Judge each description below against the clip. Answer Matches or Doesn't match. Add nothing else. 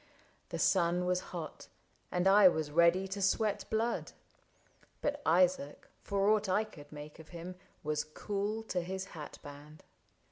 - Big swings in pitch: Doesn't match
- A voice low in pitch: Doesn't match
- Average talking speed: Matches